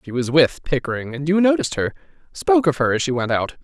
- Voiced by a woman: No, male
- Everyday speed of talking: No, fast, 230 wpm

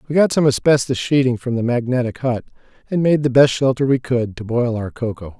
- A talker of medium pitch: No, low, 125 Hz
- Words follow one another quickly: Yes, fast, 225 wpm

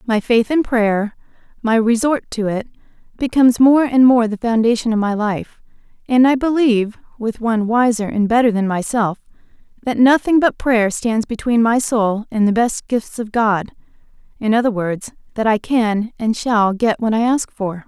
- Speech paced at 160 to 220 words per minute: Yes, average, 180 wpm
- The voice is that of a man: No, female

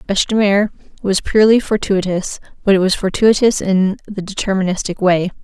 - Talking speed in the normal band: Yes, average, 155 wpm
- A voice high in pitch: Yes, high, 195 Hz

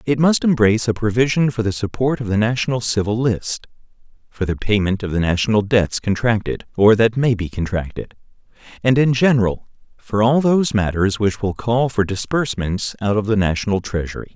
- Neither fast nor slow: Yes, average, 180 wpm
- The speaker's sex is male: Yes, male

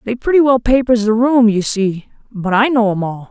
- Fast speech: Yes, fast, 235 wpm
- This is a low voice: No, high, 225 Hz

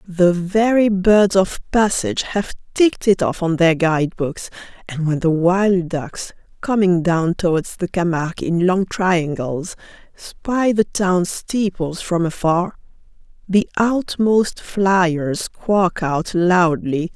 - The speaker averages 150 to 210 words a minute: No, slow, 135 wpm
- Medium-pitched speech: Yes, medium, 180 Hz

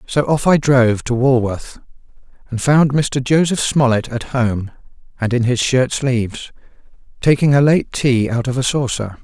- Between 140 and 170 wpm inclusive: Yes, average, 160 wpm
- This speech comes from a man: Yes, male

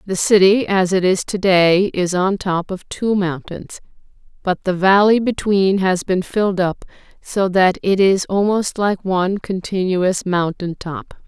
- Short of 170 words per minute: Yes, average, 160 wpm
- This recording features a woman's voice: Yes, female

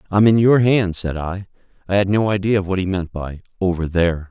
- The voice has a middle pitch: No, very low, 95 Hz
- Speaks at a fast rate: Yes, fast, 235 wpm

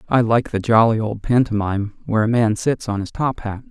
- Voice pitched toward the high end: No, low, 110 Hz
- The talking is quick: Yes, fast, 225 wpm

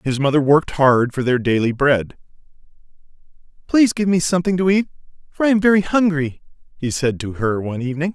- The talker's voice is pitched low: No, medium, 155 Hz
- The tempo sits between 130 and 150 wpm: No, average, 185 wpm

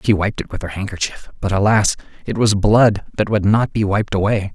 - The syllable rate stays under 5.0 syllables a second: No, 5.4 syllables/s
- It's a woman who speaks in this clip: No, male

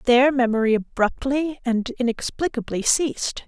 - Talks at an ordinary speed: No, slow, 105 wpm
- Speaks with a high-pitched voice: Yes, very high, 250 Hz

